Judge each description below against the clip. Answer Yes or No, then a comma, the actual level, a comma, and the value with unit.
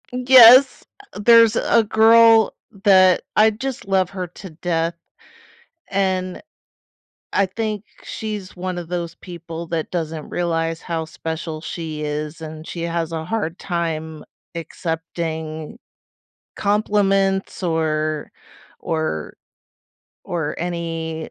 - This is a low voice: No, medium, 170 Hz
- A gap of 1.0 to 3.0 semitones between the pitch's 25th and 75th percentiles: No, average, 3.6 semitones